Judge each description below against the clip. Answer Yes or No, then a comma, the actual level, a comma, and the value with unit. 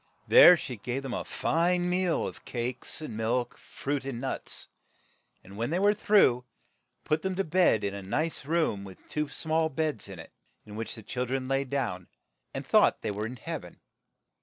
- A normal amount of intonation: No, wide, 6.3 semitones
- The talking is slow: No, average, 190 wpm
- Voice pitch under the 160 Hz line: Yes, low, 135 Hz